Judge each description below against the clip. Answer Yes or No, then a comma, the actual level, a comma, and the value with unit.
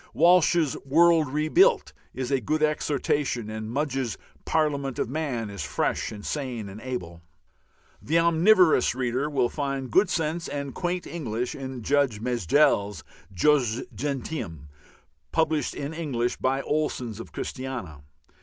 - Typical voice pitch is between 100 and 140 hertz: Yes, low, 135 Hz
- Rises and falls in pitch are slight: No, average, 4.7 semitones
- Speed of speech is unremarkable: No, slow, 130 wpm